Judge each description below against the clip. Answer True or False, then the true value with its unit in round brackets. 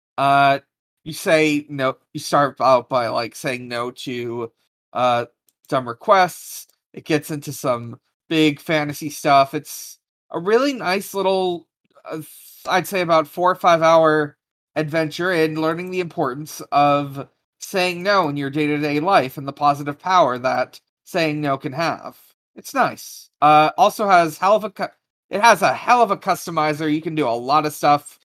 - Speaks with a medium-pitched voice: True (155 Hz)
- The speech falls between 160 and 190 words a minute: True (170 wpm)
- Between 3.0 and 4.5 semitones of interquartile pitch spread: True (3.3 semitones)